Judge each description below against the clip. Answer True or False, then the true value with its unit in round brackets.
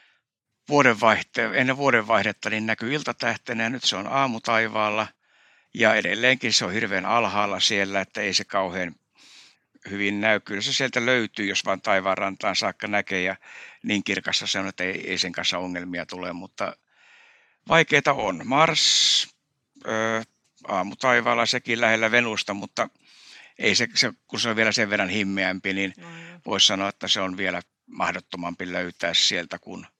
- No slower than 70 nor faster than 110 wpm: False (155 wpm)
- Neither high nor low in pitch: False (105 Hz)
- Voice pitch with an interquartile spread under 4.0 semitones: True (3.2 semitones)